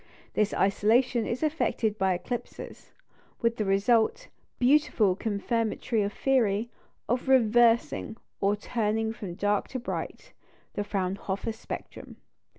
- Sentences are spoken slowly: Yes, slow, 115 wpm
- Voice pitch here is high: Yes, high, 220 Hz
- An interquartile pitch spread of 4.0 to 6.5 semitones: No, average, 2.9 semitones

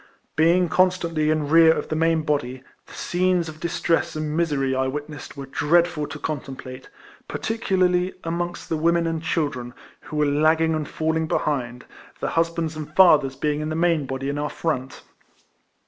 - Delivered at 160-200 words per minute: Yes, average, 165 wpm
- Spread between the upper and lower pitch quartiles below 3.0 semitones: Yes, narrow, 2.4 semitones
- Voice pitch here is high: No, medium, 155 Hz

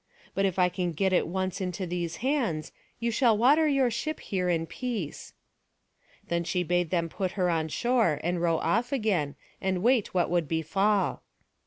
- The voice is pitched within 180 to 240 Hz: Yes, medium, 185 Hz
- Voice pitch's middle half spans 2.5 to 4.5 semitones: No, average, 5.0 semitones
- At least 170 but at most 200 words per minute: Yes, average, 180 wpm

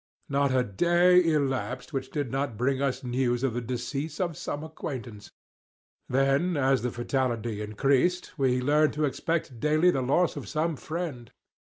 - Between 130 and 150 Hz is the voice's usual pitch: Yes, low, 135 Hz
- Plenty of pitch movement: No, average, 3.6 semitones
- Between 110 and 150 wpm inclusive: No, average, 160 wpm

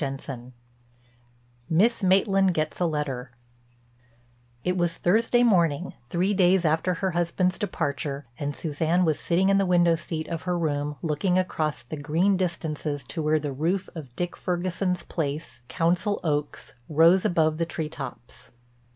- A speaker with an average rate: Yes, average, 150 wpm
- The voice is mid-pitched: Yes, medium, 165 Hz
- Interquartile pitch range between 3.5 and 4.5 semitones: Yes, average, 3.9 semitones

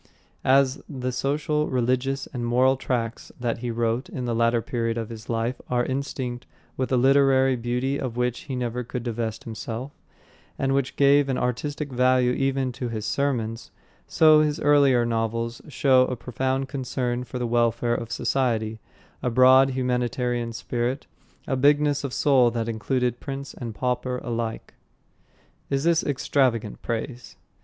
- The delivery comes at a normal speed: Yes, average, 155 wpm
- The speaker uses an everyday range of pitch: No, narrow, 2.3 semitones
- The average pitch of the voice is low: Yes, low, 125 Hz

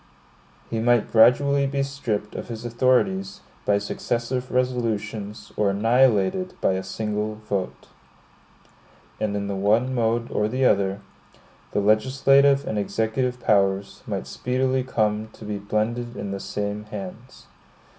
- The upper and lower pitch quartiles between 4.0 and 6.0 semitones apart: No, average, 3.6 semitones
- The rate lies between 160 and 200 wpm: No, slow, 135 wpm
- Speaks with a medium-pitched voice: No, low, 110 Hz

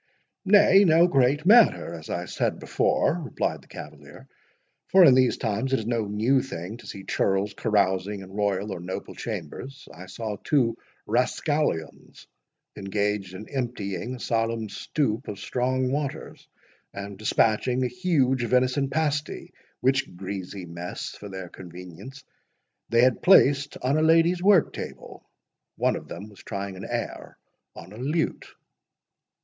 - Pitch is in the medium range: No, low, 115 Hz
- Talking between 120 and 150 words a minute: Yes, average, 145 wpm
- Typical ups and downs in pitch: No, wide, 5.7 semitones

